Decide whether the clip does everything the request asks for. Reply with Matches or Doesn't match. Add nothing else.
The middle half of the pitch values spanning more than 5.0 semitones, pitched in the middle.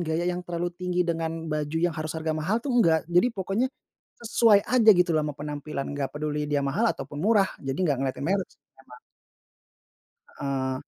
Doesn't match